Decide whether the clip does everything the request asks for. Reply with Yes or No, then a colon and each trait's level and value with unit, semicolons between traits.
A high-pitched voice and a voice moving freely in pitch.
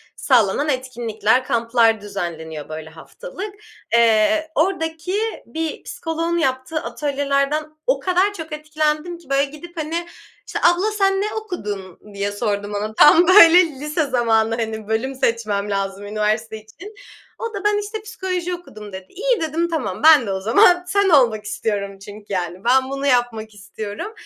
Yes: very high, 265 Hz; wide, 8.1 semitones